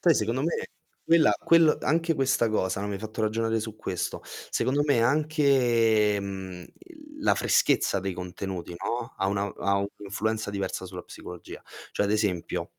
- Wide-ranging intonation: Yes, wide, 6.0 semitones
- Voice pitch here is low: Yes, low, 110 Hz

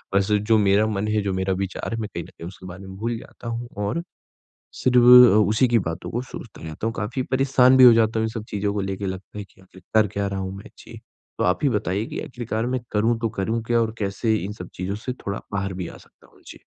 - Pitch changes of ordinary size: Yes, average, 3.0 semitones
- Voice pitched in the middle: No, low, 105 Hz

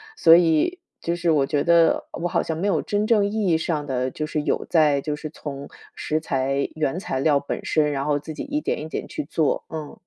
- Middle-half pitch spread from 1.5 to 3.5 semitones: Yes, average, 2.8 semitones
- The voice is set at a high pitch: No, medium, 155 Hz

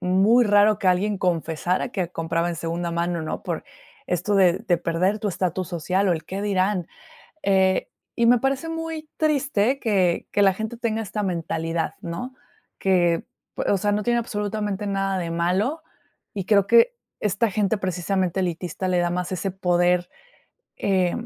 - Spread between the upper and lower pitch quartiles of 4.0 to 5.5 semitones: No, average, 3.2 semitones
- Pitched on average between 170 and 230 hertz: Yes, high, 190 Hz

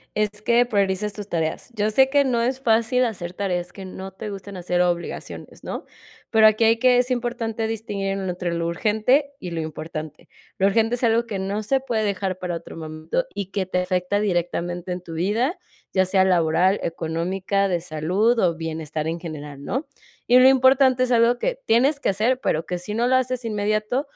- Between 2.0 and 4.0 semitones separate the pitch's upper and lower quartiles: No, average, 5.0 semitones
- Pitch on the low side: No, high, 200 Hz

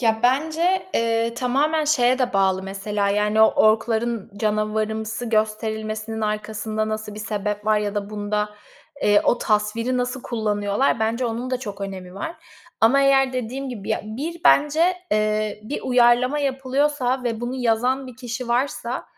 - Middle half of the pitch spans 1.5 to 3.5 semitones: Yes, average, 3.2 semitones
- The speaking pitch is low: No, high, 225 Hz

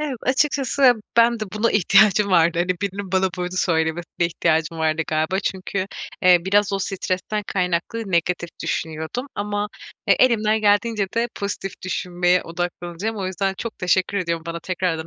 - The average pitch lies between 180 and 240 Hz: Yes, medium, 185 Hz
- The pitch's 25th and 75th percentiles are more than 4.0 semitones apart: No, average, 3.3 semitones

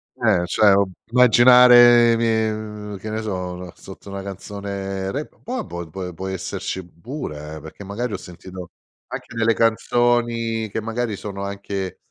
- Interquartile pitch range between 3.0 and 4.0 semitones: Yes, average, 3.4 semitones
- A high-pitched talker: No, low, 100 Hz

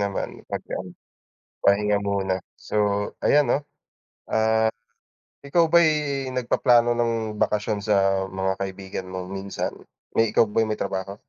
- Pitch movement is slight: No, average, 3.3 semitones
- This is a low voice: Yes, low, 105 Hz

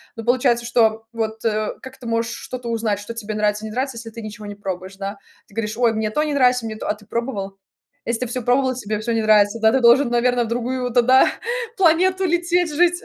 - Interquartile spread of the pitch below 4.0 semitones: Yes, average, 2.9 semitones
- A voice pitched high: Yes, high, 230 Hz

